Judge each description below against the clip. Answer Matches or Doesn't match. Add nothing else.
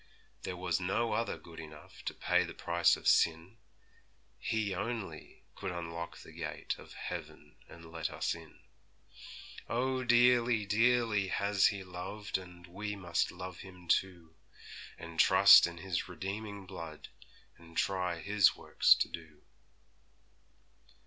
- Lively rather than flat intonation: Doesn't match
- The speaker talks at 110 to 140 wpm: Matches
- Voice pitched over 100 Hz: Doesn't match